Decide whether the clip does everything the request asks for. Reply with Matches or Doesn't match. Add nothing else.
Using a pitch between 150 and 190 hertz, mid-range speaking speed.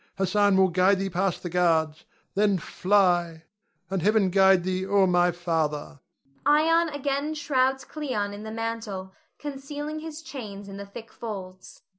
Doesn't match